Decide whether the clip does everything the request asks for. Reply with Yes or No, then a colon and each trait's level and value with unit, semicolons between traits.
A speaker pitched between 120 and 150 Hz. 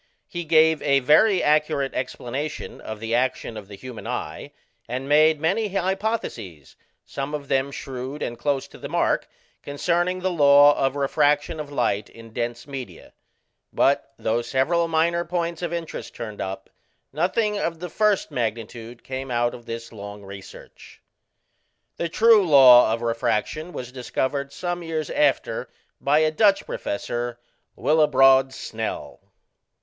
Yes: medium, 140 Hz